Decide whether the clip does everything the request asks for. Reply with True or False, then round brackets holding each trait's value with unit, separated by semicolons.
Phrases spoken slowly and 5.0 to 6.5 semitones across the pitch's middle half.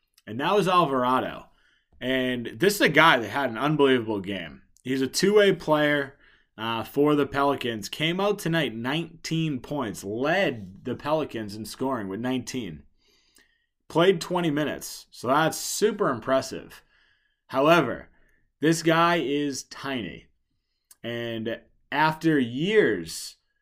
True (125 wpm; 5.5 semitones)